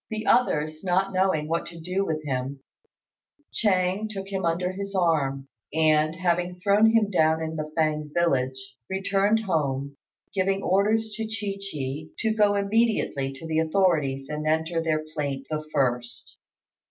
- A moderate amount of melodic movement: Yes, average, 4.4 semitones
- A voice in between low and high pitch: Yes, medium, 165 Hz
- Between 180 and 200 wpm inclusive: No, average, 155 wpm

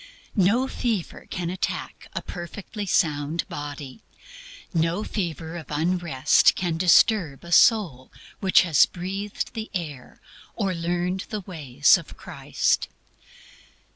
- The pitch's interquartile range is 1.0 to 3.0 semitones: No, average, 3.7 semitones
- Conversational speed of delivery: No, slow, 115 wpm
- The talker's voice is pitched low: No, medium, 175 Hz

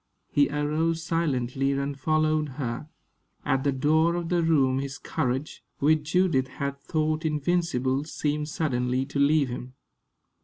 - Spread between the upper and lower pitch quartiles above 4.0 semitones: No, average, 2.9 semitones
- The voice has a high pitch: No, medium, 145 Hz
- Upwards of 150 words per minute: No, average, 140 wpm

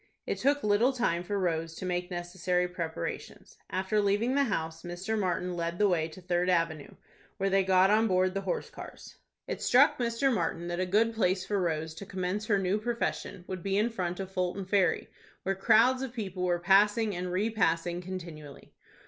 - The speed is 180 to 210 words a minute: Yes, average, 190 wpm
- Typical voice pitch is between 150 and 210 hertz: Yes, medium, 185 Hz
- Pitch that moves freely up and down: No, average, 3.0 semitones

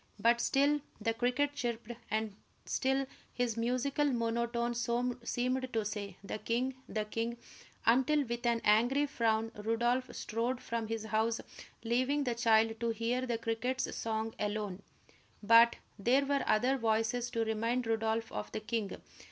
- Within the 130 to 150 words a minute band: Yes, average, 145 wpm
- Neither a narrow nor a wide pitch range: No, narrow, 2.0 semitones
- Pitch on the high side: Yes, high, 235 Hz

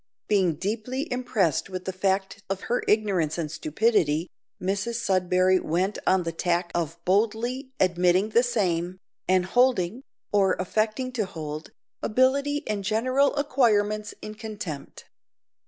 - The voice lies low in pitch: No, high, 200 Hz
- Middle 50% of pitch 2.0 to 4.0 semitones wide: No, average, 4.4 semitones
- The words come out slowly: Yes, slow, 130 wpm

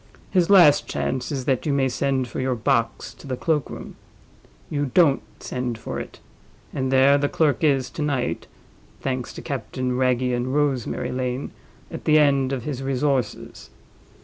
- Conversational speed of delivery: Yes, average, 160 wpm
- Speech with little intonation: Yes, narrow, 2.2 semitones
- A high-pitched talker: No, low, 135 Hz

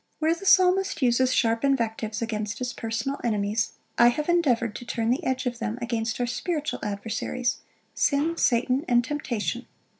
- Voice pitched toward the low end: No, high, 240 Hz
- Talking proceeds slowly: No, average, 160 wpm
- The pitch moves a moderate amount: Yes, average, 3.7 semitones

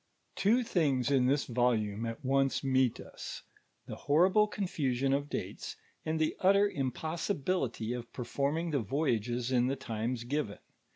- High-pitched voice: No, low, 135 Hz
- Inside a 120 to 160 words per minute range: Yes, average, 140 wpm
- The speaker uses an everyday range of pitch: Yes, average, 4.4 semitones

